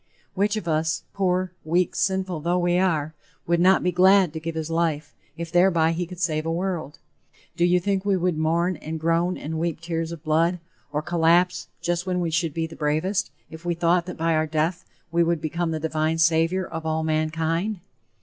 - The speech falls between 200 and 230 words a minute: Yes, fast, 205 wpm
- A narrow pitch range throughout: Yes, narrow, 2.0 semitones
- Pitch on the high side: No, medium, 170 Hz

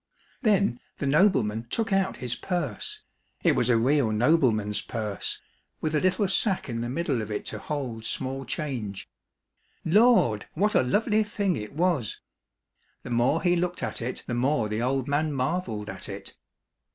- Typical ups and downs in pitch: No, wide, 7.5 semitones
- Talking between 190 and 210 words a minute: No, average, 165 wpm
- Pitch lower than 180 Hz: Yes, low, 135 Hz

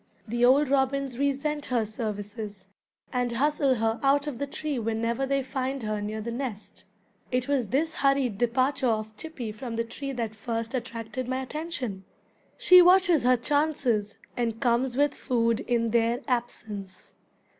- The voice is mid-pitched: No, high, 245 Hz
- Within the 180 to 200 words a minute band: No, average, 155 wpm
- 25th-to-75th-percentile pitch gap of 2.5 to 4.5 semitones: Yes, average, 3.4 semitones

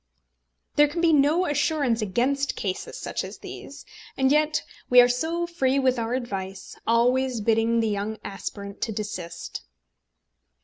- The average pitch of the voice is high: Yes, high, 245 Hz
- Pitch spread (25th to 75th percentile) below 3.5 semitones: No, average, 4.9 semitones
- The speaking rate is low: No, average, 150 wpm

